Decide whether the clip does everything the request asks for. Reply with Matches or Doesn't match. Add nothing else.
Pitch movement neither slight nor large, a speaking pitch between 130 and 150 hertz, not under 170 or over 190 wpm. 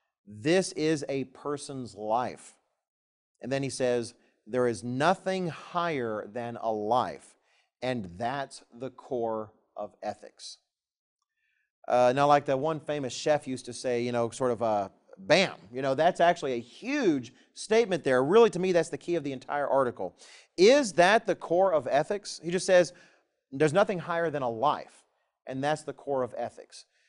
Doesn't match